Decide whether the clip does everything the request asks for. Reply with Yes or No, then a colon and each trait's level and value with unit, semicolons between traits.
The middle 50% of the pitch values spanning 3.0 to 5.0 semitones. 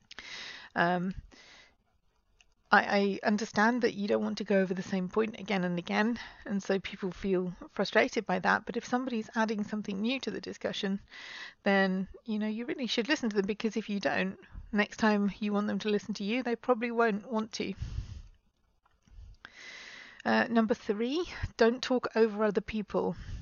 No: narrow, 2.6 semitones